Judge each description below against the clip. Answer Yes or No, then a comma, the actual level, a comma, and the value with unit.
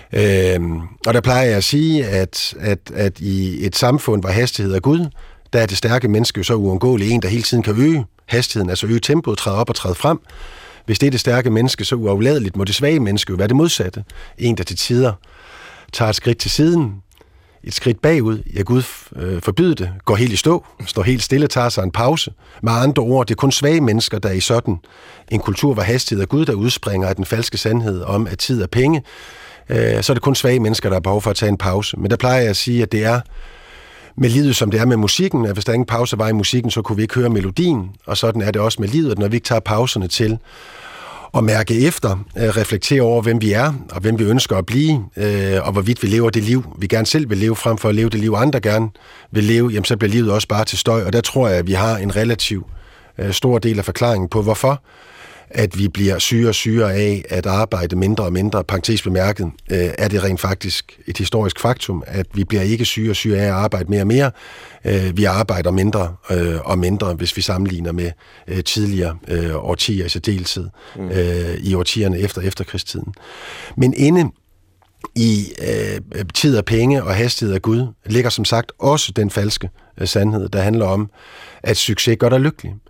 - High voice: No, low, 110 Hz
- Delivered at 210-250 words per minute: Yes, fast, 225 wpm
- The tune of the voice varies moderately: Yes, average, 3.7 semitones